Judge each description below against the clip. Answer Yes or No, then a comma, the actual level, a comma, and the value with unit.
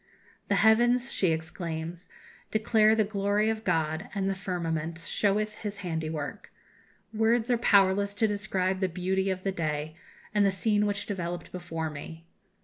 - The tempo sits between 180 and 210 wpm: No, average, 150 wpm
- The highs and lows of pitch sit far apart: No, average, 4.1 semitones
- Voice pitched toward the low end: No, high, 195 Hz